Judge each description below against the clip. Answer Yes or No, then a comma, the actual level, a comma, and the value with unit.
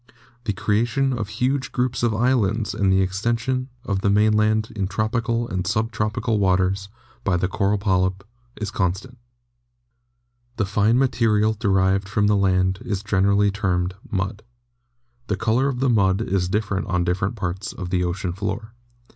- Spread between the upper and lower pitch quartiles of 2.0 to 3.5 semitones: Yes, average, 2.9 semitones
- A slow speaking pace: No, average, 155 wpm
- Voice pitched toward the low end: Yes, low, 105 Hz